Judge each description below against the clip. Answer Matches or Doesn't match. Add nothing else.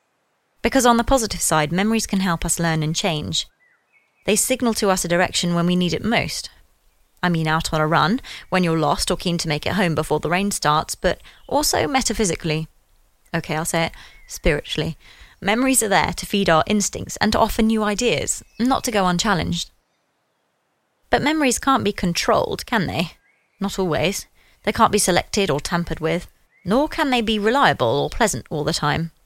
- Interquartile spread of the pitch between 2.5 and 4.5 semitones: Doesn't match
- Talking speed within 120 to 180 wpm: Doesn't match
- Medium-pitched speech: Matches